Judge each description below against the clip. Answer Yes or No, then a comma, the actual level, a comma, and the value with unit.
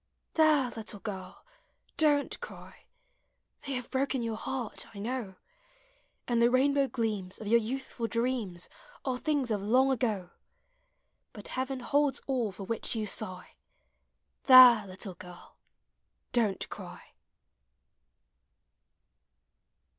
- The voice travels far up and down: No, average, 4.2 semitones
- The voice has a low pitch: No, high, 235 Hz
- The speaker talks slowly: Yes, slow, 115 wpm